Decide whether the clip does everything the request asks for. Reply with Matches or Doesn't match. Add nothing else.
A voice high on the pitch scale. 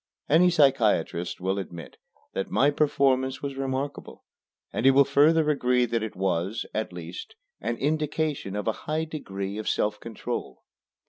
Doesn't match